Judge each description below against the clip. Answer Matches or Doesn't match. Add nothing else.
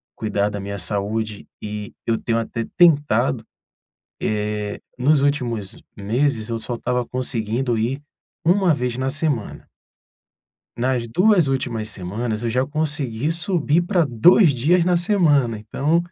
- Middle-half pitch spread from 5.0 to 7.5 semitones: Matches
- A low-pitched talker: Matches